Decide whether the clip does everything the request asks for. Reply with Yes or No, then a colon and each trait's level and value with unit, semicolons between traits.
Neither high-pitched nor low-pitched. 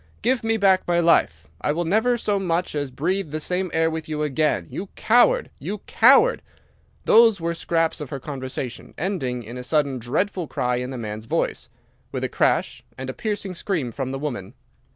Yes: medium, 160 Hz